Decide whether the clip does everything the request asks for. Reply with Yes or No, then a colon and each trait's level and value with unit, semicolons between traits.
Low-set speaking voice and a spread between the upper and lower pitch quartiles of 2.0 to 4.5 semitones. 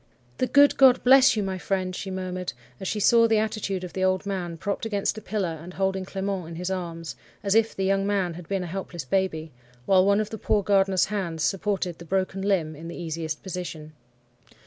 No: high, 190 Hz; narrow, 2.5 semitones